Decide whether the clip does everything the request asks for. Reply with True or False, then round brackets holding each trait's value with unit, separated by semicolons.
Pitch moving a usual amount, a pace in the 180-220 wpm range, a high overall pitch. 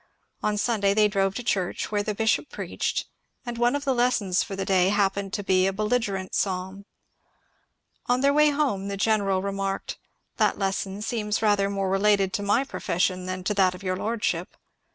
False (2.2 semitones; 190 wpm; 200 Hz)